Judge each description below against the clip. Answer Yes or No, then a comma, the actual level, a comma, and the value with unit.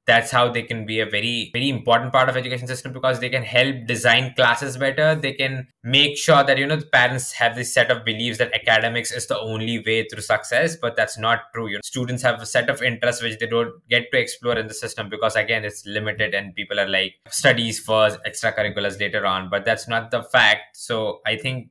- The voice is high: No, low, 115 Hz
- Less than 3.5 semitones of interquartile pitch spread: Yes, average, 2.8 semitones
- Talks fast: Yes, fast, 230 wpm